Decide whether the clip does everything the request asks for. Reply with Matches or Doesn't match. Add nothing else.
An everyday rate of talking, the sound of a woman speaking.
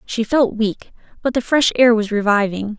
Matches